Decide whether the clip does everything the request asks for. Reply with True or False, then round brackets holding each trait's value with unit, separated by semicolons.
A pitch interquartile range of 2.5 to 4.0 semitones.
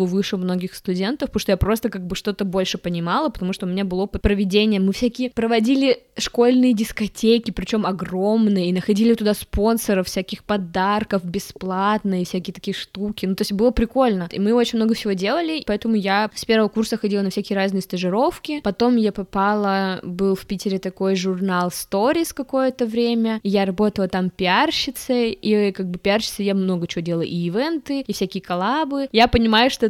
True (3.2 semitones)